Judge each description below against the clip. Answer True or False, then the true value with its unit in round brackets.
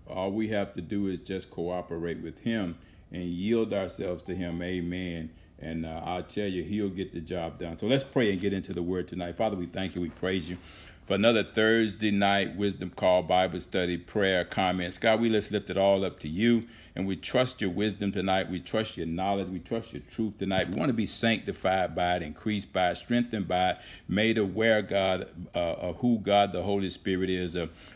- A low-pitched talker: True (95 Hz)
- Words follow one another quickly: True (220 wpm)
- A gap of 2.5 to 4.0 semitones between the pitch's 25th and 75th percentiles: True (2.8 semitones)